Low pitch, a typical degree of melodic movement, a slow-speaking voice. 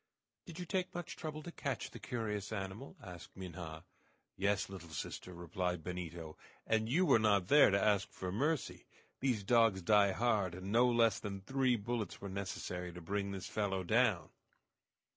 No: low, 100 Hz; average, 4.5 semitones; average, 170 wpm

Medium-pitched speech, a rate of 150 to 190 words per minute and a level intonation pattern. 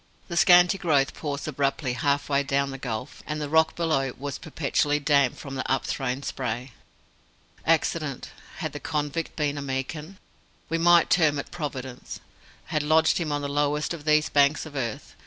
Yes: medium, 145 Hz; average, 175 wpm; narrow, 2.3 semitones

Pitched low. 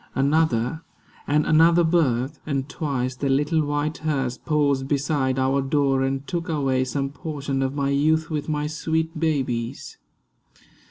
No: medium, 145 Hz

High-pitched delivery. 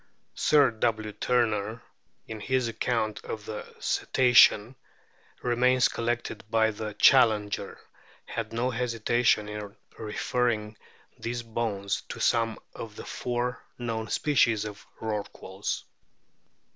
No: low, 115 Hz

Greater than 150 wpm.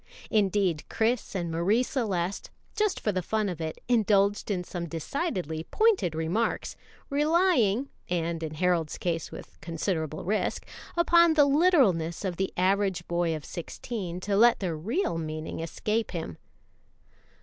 No: average, 145 wpm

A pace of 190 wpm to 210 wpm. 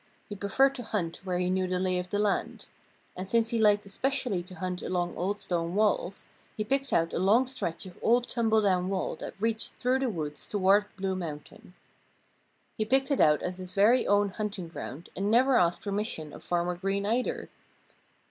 Yes: average, 195 wpm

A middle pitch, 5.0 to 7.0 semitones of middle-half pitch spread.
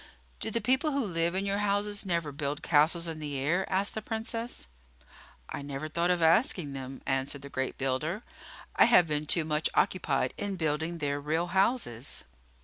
Yes: medium, 165 Hz; wide, 5.5 semitones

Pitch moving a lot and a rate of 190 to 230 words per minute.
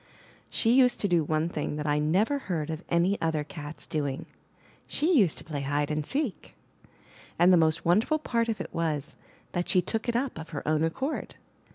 Yes: wide, 6.6 semitones; average, 200 wpm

